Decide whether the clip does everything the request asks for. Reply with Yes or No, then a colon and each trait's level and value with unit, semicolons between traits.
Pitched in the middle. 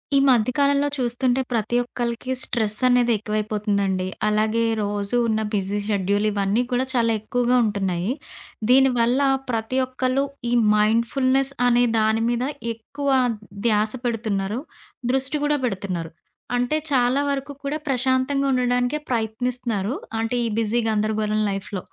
No: high, 235 Hz